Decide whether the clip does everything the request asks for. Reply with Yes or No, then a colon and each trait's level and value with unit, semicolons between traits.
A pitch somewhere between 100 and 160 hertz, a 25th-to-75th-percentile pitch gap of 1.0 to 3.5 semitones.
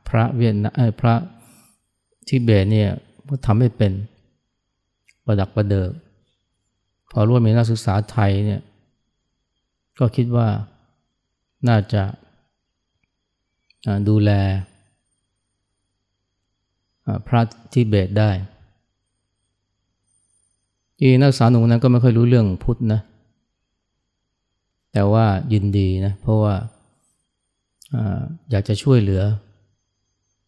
Yes: low, 105 Hz; average, 2.8 semitones